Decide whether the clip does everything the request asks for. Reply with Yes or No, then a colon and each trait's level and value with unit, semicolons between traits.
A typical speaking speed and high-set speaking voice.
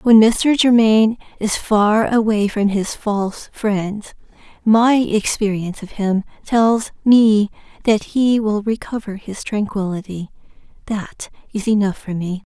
No: slow, 130 wpm; high, 210 Hz